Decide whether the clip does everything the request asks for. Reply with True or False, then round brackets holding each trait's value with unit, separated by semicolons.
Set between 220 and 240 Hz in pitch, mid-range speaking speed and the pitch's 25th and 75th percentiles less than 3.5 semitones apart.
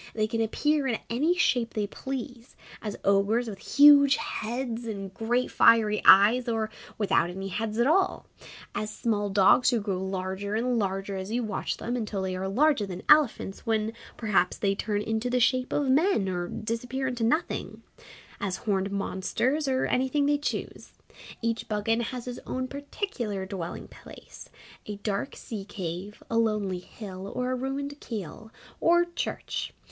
False (225 Hz; 165 wpm; 4.2 semitones)